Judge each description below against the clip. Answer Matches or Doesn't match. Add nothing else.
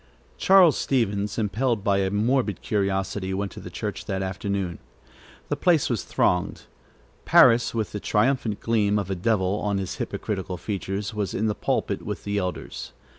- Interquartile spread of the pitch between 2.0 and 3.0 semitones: Matches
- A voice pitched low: Matches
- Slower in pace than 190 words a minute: Matches